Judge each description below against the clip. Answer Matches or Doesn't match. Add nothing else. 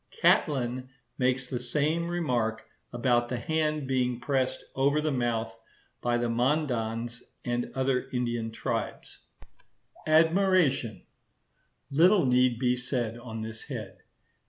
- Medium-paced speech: Doesn't match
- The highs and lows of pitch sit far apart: Doesn't match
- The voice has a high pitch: Doesn't match